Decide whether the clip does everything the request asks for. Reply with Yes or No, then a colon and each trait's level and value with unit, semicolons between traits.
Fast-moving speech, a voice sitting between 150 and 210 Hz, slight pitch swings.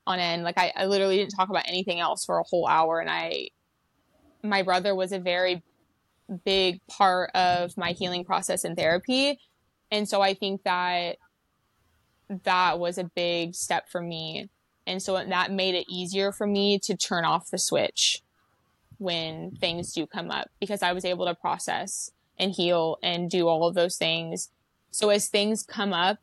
No: average, 180 wpm; medium, 185 Hz; narrow, 2.3 semitones